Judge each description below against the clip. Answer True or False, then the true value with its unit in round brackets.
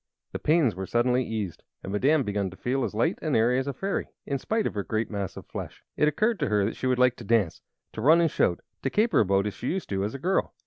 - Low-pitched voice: True (125 Hz)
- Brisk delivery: True (280 wpm)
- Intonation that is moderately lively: False (6.5 semitones)